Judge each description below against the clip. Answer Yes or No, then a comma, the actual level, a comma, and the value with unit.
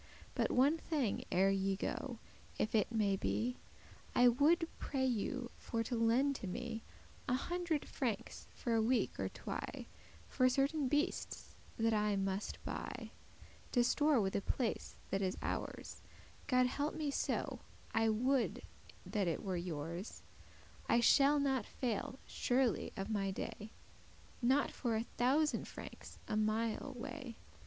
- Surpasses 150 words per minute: No, average, 145 wpm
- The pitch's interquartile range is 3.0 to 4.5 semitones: Yes, average, 4.2 semitones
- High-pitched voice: Yes, high, 240 Hz